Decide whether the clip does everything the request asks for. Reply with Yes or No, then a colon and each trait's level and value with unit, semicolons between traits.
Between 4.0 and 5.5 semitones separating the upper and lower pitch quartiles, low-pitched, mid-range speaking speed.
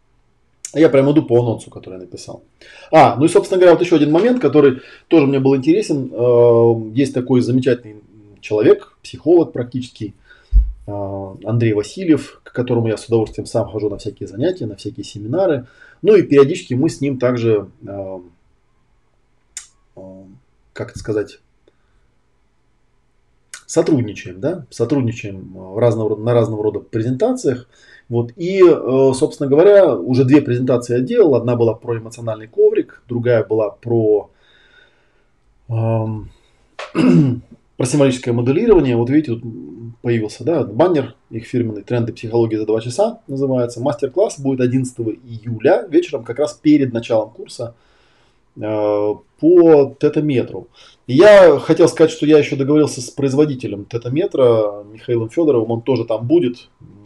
Yes: average, 4.7 semitones; low, 120 Hz; average, 130 wpm